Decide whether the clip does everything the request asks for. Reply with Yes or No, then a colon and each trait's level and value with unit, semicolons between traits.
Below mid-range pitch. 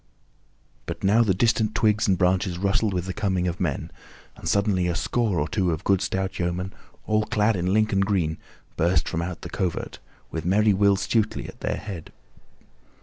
Yes: very low, 95 Hz